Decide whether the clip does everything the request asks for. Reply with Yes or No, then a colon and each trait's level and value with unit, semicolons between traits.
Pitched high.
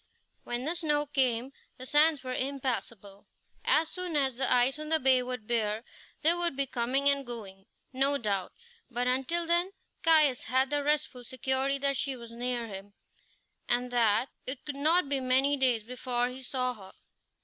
Yes: very high, 260 Hz